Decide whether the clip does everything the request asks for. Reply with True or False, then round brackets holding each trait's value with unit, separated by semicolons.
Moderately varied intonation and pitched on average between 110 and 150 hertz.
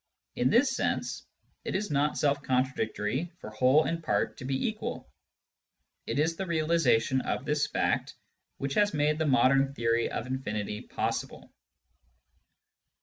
True (3.8 semitones; 140 Hz)